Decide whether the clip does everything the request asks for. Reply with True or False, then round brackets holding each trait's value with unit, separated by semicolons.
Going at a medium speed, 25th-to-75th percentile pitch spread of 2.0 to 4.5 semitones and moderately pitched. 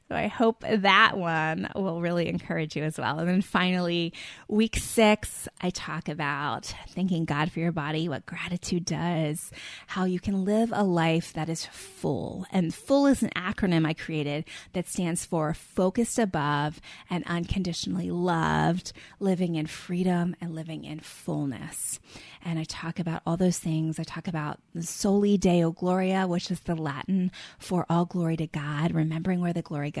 True (170 wpm; 2.7 semitones; 170 Hz)